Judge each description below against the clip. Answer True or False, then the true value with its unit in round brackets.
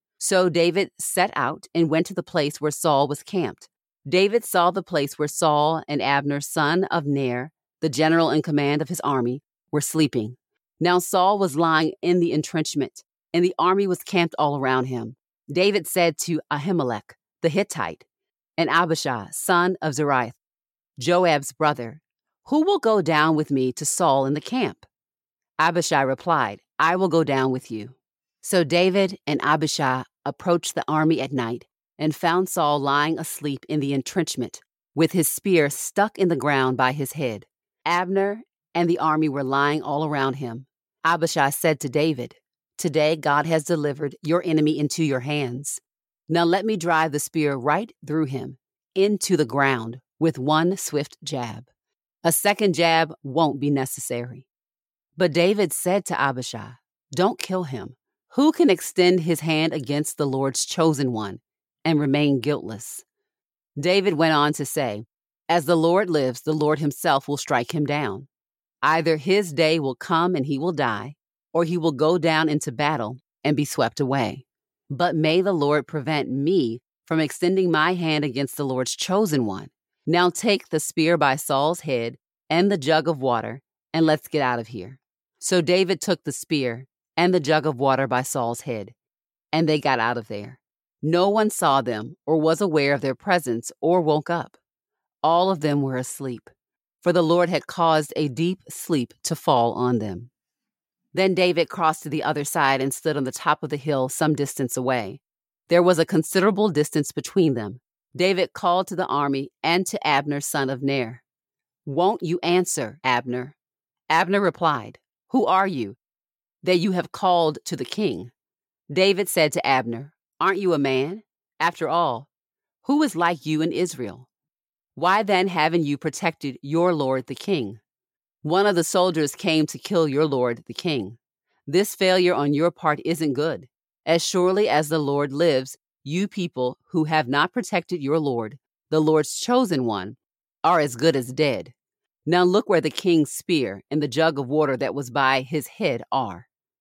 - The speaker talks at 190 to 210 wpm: False (175 wpm)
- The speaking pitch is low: False (155 Hz)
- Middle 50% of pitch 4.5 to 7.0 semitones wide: False (4.1 semitones)